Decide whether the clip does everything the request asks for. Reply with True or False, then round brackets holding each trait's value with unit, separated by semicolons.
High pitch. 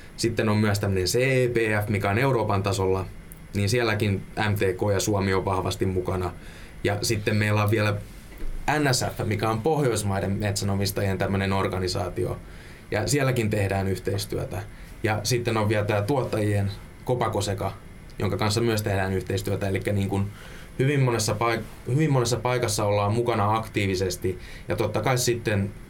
False (105 Hz)